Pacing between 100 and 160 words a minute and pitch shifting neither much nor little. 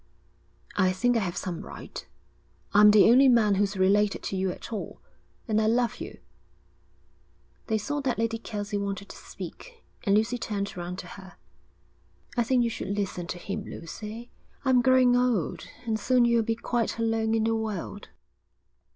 No: average, 170 wpm; average, 3.1 semitones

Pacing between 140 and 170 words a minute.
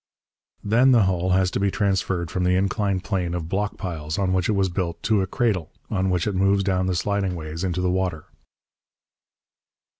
No: average, 200 wpm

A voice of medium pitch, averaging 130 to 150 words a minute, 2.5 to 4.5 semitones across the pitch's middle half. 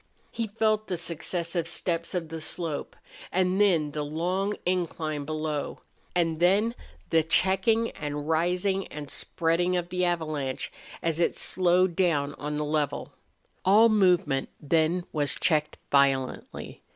Yes: medium, 170 Hz; slow, 135 wpm; average, 3.3 semitones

